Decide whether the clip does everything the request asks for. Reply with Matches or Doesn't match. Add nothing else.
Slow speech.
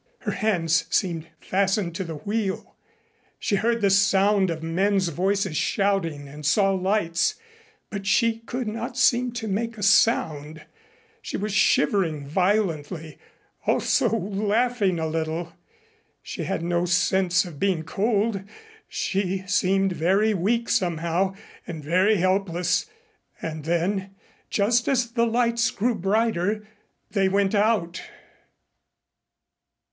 Matches